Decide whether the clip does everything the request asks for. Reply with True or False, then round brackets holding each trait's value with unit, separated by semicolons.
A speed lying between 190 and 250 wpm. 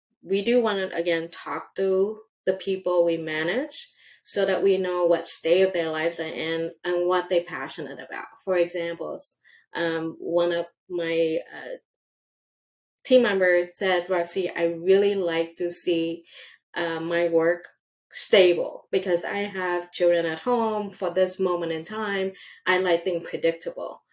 False (155 wpm)